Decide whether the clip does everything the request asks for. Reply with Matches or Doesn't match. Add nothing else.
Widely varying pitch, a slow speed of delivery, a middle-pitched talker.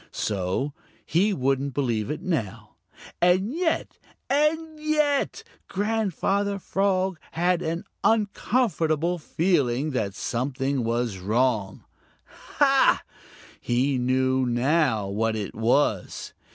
Matches